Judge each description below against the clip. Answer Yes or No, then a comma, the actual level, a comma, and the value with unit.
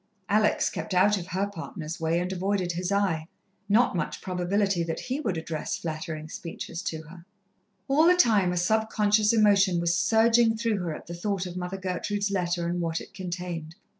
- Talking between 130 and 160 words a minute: No, average, 185 wpm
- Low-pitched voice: No, medium, 185 Hz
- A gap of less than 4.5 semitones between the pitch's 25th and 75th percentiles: Yes, average, 3.3 semitones